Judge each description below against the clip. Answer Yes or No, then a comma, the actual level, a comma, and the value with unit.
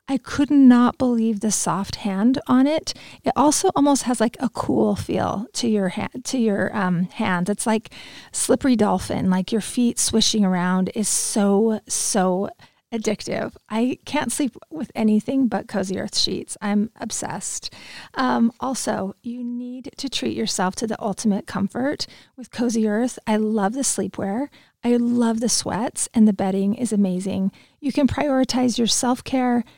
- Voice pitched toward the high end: Yes, high, 225 Hz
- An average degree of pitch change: Yes, average, 3.6 semitones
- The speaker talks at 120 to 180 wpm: Yes, average, 165 wpm